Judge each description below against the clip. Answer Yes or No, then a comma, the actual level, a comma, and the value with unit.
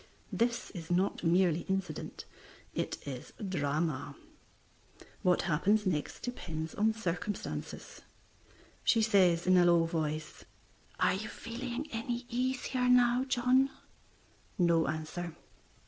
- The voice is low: No, medium, 185 Hz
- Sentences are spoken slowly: Yes, slow, 110 wpm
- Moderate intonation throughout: No, wide, 6.2 semitones